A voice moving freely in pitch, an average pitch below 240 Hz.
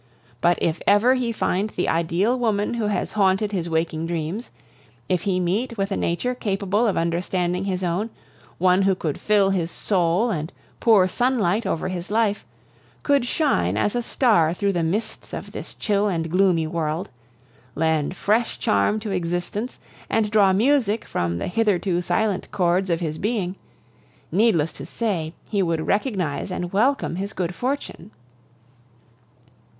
No: average, 3.9 semitones; high, 190 Hz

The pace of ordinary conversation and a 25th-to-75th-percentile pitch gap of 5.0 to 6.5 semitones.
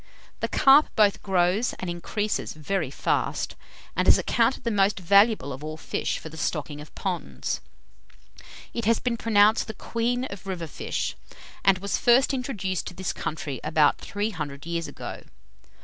Yes: average, 165 wpm; wide, 5.6 semitones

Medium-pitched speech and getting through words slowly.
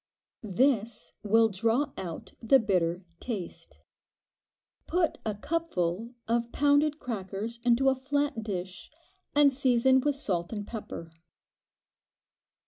No: high, 230 Hz; slow, 110 wpm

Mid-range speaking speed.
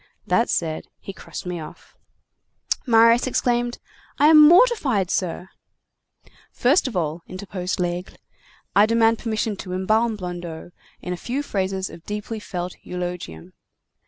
No: slow, 130 wpm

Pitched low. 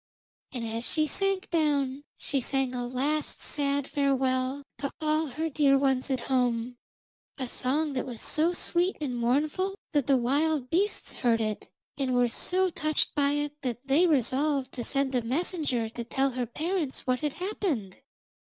No: very high, 275 Hz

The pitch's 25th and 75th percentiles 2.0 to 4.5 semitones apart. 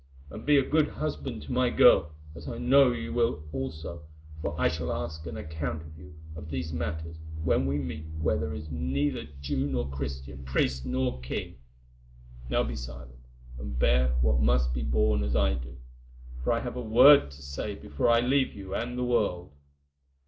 No: average, 4.9 semitones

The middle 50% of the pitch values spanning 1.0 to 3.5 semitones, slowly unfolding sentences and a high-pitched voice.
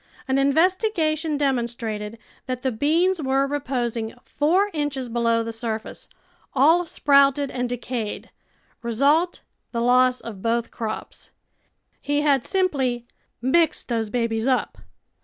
No: average, 3.9 semitones; slow, 125 wpm; very high, 260 Hz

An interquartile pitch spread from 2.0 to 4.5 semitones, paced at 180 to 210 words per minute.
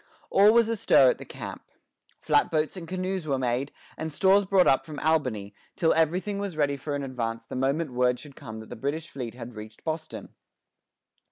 No: average, 5.2 semitones; average, 195 wpm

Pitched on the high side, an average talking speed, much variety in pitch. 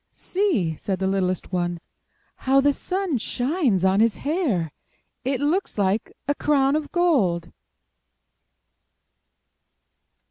No: very high, 250 Hz; slow, 110 wpm; wide, 8.1 semitones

